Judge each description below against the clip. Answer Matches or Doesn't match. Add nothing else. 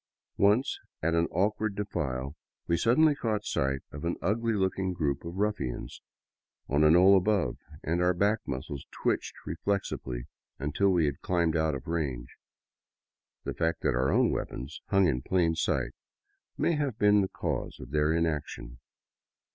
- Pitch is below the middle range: Matches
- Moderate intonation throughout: Doesn't match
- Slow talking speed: Doesn't match